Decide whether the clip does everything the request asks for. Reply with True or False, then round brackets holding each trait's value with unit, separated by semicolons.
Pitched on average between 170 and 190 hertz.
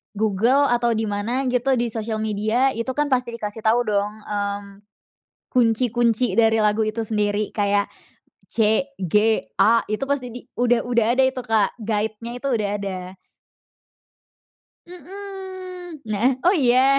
False (230 Hz)